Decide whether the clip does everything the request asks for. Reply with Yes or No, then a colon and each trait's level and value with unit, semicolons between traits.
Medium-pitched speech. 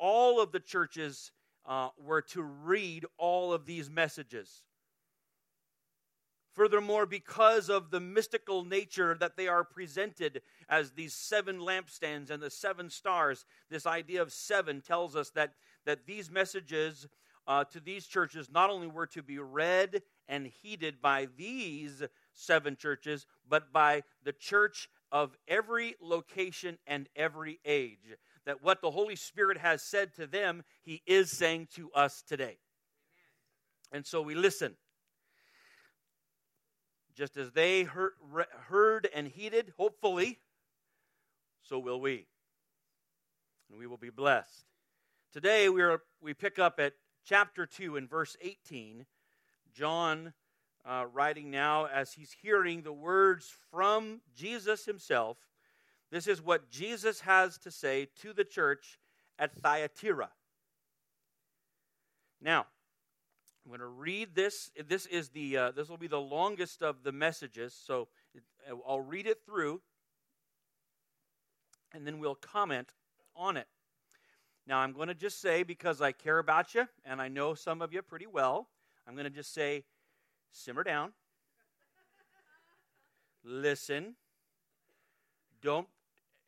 Yes: medium, 165 Hz